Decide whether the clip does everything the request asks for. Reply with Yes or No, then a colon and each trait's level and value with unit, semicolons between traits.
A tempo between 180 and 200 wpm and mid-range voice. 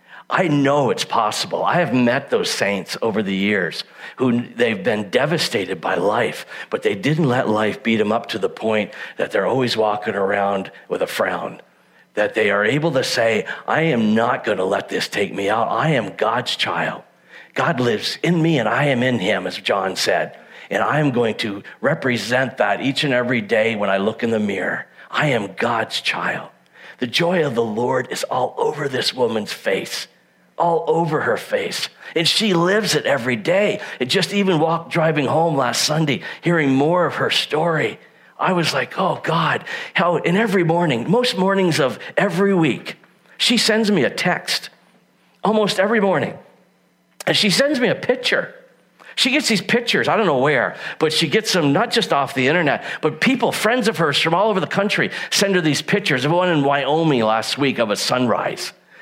Yes: average, 195 wpm; medium, 160 Hz